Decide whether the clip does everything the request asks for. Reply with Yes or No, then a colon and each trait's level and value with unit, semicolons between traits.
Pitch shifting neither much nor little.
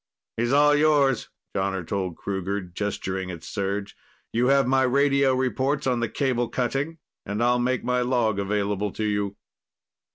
Yes: average, 4.9 semitones